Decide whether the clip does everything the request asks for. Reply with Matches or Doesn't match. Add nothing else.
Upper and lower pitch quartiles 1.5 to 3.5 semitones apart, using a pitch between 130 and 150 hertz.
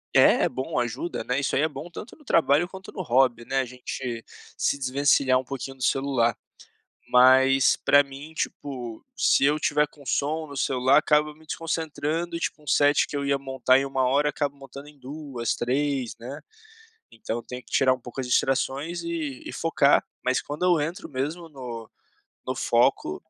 Matches